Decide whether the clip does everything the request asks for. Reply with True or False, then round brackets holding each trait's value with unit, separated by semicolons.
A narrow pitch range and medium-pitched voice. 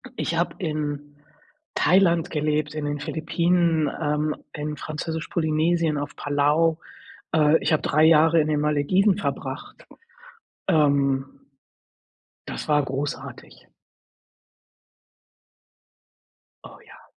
True (1.9 semitones; 155 Hz)